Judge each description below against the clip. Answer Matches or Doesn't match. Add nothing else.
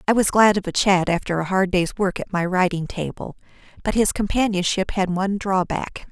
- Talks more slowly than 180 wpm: Doesn't match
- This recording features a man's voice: Doesn't match